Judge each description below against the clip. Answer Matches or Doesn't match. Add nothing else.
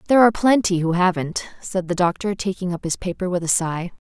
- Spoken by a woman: Matches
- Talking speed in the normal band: Doesn't match